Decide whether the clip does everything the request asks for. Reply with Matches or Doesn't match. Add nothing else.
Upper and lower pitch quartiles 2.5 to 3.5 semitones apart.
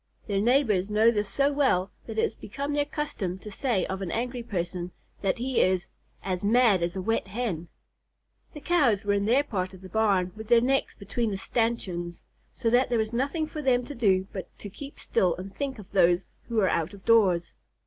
Doesn't match